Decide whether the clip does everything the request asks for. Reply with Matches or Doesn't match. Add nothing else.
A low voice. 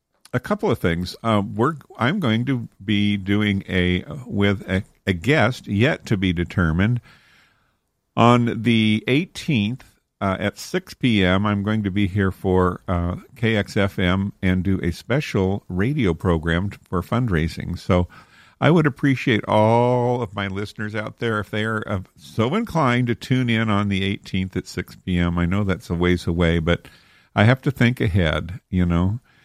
Matches